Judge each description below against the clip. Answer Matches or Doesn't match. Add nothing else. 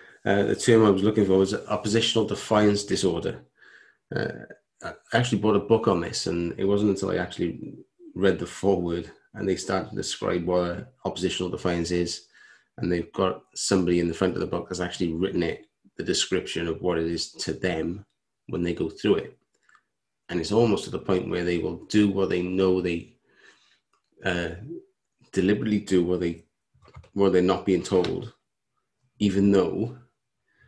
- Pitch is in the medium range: Doesn't match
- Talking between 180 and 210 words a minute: Doesn't match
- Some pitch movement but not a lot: Matches